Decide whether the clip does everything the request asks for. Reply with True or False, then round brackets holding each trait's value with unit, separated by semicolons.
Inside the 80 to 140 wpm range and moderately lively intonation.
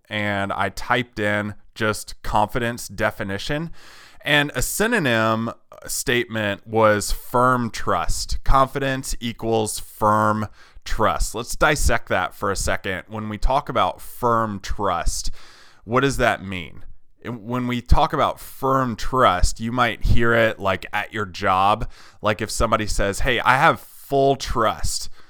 True (135 wpm; 3.2 semitones)